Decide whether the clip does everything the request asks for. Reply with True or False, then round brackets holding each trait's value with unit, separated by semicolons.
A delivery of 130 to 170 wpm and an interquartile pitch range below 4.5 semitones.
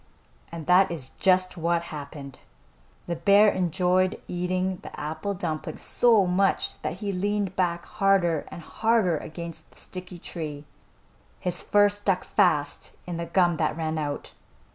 True (145 wpm; 2.9 semitones)